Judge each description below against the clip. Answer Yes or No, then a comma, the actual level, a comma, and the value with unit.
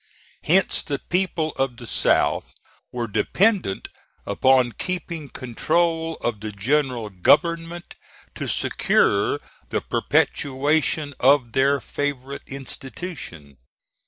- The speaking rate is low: Yes, slow, 100 wpm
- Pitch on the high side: No, medium, 140 Hz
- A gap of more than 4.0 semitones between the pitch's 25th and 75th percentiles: Yes, average, 5.1 semitones